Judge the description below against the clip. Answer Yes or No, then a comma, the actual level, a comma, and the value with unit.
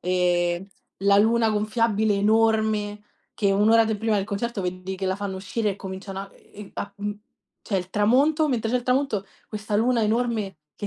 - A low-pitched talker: No, high, 210 Hz